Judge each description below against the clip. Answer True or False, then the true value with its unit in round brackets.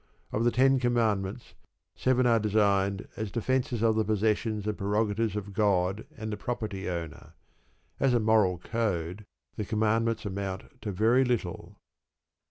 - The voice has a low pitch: True (110 Hz)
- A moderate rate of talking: True (145 wpm)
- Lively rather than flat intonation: False (2.6 semitones)